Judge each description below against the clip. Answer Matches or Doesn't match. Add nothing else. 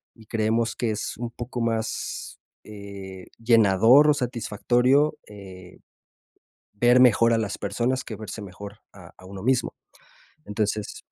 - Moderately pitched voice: Doesn't match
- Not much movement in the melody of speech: Doesn't match